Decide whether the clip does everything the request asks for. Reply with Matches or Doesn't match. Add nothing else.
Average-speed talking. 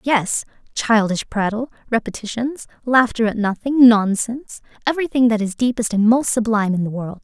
Matches